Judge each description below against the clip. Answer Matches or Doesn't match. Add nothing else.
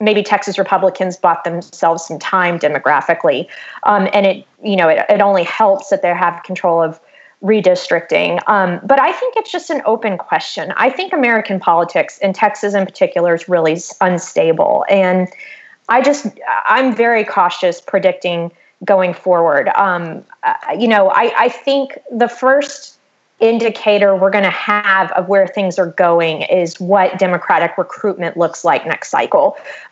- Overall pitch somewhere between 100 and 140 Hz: Doesn't match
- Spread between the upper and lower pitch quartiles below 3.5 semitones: Doesn't match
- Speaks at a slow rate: Doesn't match